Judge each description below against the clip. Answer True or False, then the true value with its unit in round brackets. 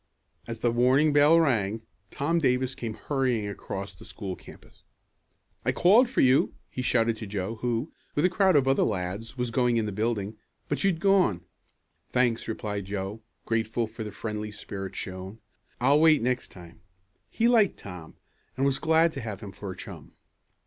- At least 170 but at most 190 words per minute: True (175 wpm)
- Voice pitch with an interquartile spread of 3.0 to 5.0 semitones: False (5.4 semitones)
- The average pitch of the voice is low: True (115 Hz)